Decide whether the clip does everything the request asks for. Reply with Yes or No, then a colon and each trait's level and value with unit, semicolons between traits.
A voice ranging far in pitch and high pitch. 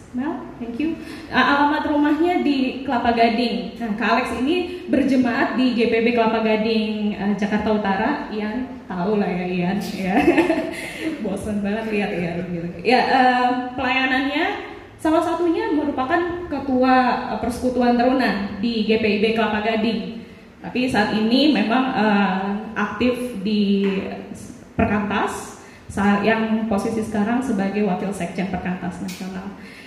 No: average, 3.8 semitones; high, 230 Hz